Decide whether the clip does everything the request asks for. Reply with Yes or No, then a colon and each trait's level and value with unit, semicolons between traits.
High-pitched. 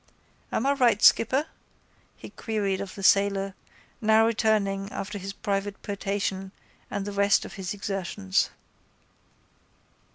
Yes: high, 200 Hz